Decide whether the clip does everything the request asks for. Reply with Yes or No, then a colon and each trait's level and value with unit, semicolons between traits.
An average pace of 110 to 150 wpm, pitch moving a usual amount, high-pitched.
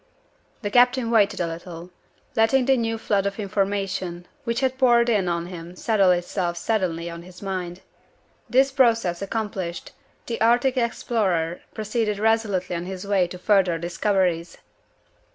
Yes: average, 145 wpm; average, 4.3 semitones; high, 195 Hz